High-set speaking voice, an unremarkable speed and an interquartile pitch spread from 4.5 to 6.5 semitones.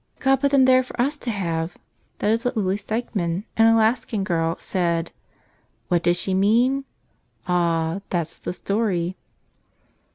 Yes: high, 200 Hz; average, 150 wpm; average, 5.2 semitones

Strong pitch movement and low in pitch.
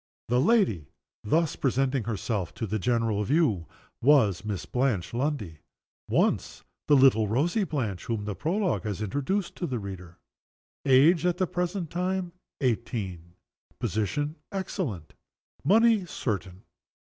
Yes: wide, 8.4 semitones; low, 125 Hz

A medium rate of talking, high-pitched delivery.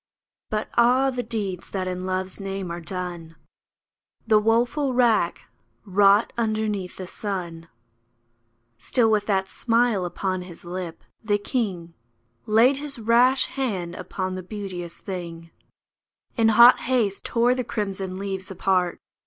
No: slow, 130 wpm; high, 200 Hz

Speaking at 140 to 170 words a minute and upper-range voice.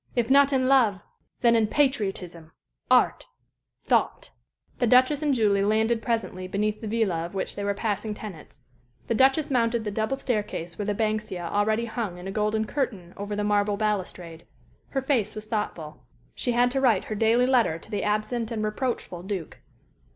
No: average, 180 wpm; high, 215 Hz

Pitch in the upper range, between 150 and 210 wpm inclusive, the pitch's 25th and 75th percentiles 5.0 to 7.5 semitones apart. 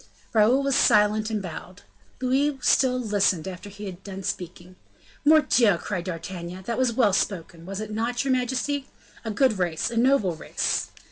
Yes: high, 210 Hz; average, 165 wpm; average, 5.3 semitones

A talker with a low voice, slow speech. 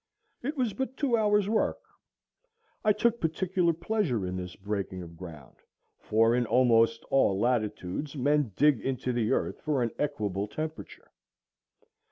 No: low, 130 Hz; average, 145 wpm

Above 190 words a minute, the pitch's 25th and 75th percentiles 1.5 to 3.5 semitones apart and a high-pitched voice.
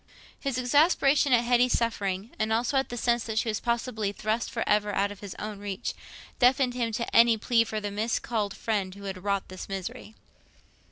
No: average, 185 wpm; average, 2.9 semitones; high, 220 Hz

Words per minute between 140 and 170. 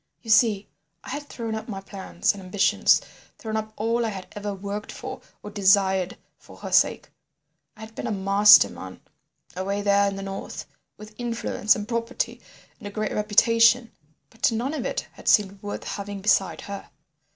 No: average, 180 wpm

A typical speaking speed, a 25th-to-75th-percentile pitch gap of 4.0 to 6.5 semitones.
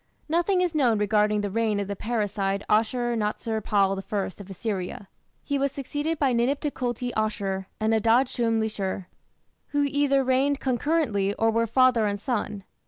Yes: average, 165 wpm; average, 4.6 semitones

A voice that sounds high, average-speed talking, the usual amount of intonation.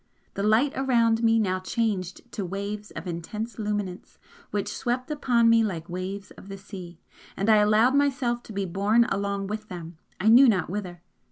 Yes: high, 210 Hz; average, 180 wpm; average, 3.4 semitones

